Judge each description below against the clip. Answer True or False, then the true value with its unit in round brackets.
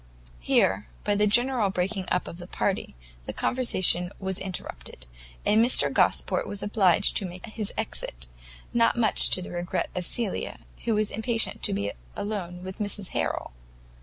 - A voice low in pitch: False (195 Hz)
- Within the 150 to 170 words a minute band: True (165 wpm)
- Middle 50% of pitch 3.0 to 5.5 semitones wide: True (3.4 semitones)